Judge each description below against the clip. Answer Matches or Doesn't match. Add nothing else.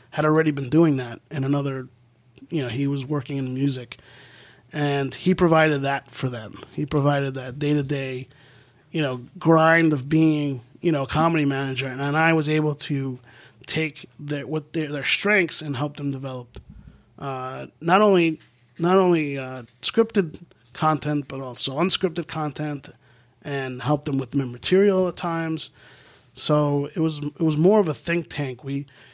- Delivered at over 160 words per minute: Matches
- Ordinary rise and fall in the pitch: Matches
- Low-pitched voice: Doesn't match